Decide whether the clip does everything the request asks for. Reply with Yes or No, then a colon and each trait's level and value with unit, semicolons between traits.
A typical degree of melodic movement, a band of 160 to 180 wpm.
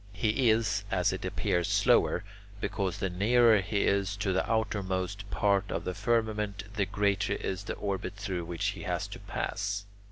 No: narrow, 2.0 semitones; average, 170 wpm